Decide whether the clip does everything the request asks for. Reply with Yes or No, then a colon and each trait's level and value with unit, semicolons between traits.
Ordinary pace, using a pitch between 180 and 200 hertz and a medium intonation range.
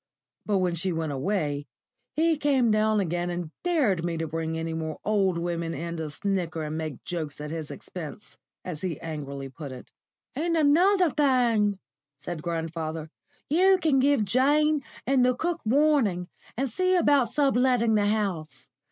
No: average, 165 wpm; high, 190 Hz; wide, 8.7 semitones